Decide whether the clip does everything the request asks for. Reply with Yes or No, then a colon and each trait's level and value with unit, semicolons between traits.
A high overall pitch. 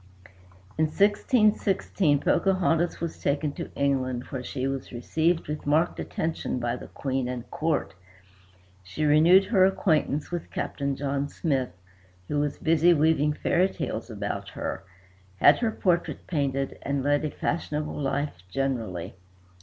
No: medium, 150 Hz